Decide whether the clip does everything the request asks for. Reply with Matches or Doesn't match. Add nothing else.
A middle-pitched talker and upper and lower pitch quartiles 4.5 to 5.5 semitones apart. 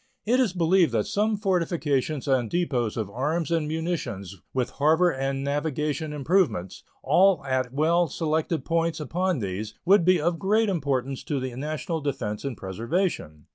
Matches